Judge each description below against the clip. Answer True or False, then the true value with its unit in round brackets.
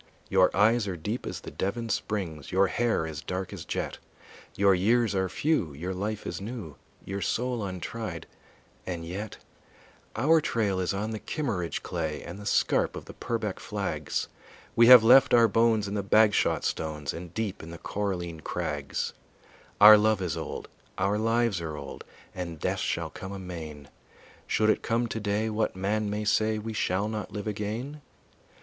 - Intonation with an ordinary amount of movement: True (3.6 semitones)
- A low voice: True (100 Hz)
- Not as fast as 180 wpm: True (170 wpm)